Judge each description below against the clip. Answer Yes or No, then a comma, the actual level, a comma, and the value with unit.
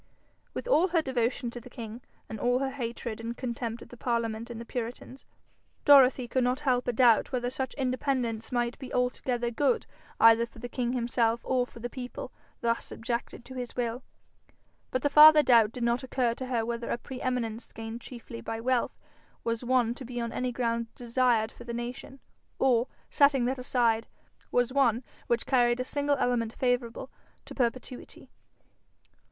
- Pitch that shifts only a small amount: Yes, narrow, 1.6 semitones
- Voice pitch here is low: No, high, 245 Hz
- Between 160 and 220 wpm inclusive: Yes, average, 180 wpm